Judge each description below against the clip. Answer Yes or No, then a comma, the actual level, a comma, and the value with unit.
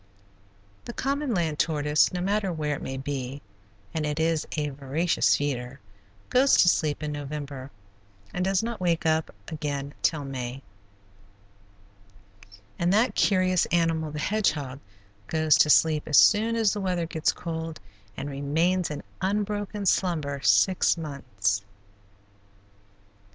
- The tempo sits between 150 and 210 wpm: No, slow, 135 wpm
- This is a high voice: No, medium, 160 Hz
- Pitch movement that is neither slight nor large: Yes, average, 4.4 semitones